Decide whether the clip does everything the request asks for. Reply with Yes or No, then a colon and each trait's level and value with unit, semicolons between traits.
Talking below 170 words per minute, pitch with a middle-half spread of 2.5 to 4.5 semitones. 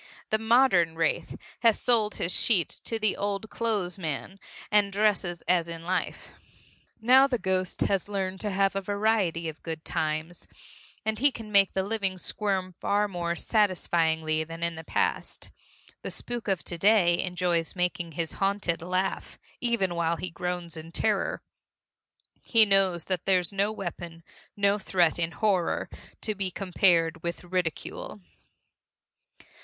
Yes: average, 150 wpm; average, 3.3 semitones